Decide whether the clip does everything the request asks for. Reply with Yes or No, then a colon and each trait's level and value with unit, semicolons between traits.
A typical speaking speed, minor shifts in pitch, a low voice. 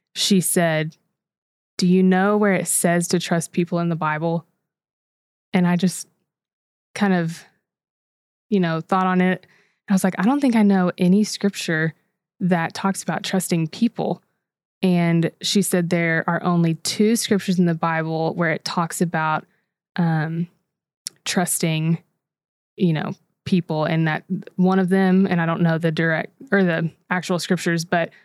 No: average, 160 wpm; narrow, 2.3 semitones; medium, 180 Hz